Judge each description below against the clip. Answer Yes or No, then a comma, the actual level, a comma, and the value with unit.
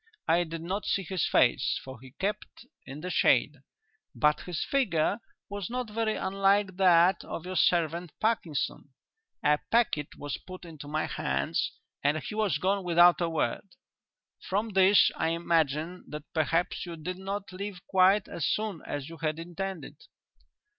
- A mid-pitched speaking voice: Yes, medium, 175 Hz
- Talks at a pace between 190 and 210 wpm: No, average, 160 wpm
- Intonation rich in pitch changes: No, average, 3.8 semitones